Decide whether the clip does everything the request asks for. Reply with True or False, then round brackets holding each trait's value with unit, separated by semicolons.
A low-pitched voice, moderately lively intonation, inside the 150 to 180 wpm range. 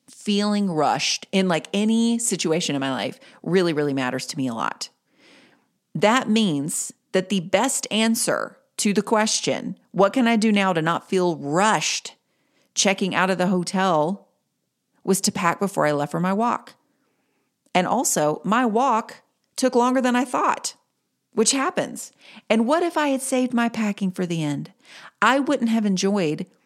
False (205 Hz; 4.8 semitones; 165 wpm)